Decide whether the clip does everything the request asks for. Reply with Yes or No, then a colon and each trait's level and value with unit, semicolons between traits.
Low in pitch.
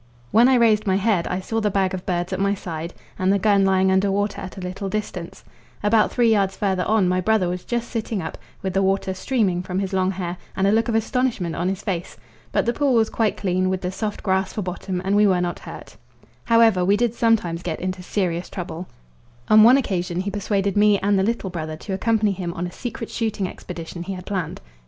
No: high, 195 Hz